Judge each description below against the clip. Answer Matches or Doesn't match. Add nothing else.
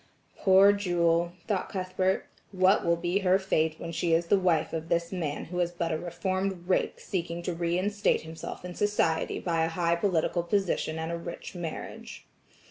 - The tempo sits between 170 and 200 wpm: Matches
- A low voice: Doesn't match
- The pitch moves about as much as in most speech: Doesn't match